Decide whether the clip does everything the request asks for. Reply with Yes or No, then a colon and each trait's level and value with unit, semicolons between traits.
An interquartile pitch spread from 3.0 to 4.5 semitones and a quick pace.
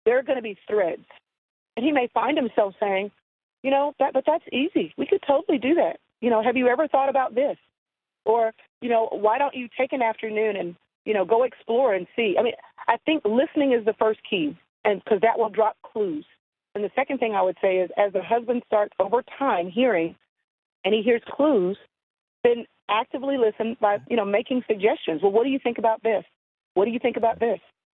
Yes: average, 4.0 semitones; fast, 220 wpm